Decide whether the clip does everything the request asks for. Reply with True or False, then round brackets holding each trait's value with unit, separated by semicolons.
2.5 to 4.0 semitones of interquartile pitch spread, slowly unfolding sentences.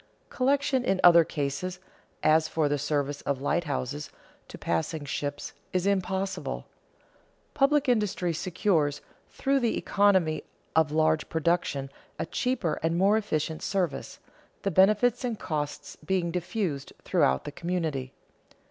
False (5.2 semitones; 125 wpm)